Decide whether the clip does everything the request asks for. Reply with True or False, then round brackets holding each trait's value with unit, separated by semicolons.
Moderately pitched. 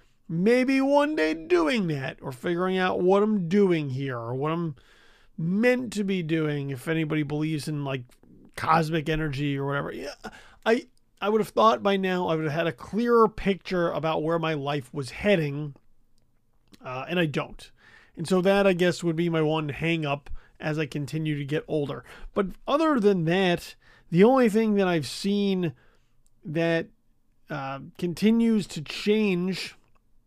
True (165 Hz)